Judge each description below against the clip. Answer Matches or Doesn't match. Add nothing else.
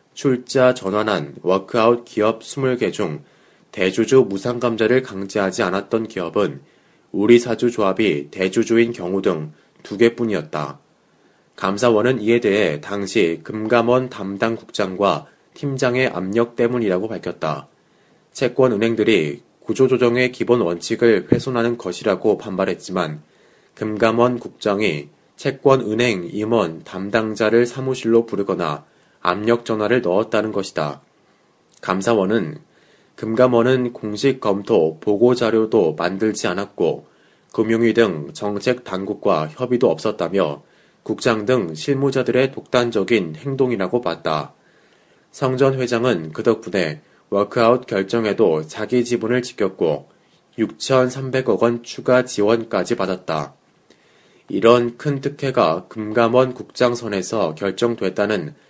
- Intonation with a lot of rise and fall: Doesn't match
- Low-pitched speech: Matches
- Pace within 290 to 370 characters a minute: Doesn't match